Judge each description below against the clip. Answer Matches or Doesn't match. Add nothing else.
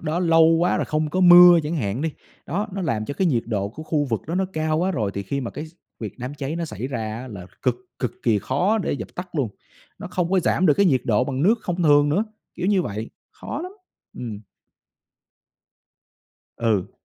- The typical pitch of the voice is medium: Matches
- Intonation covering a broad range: Matches